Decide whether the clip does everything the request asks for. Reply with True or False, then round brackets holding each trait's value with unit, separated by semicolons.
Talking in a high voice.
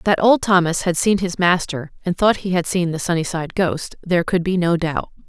False (180 Hz)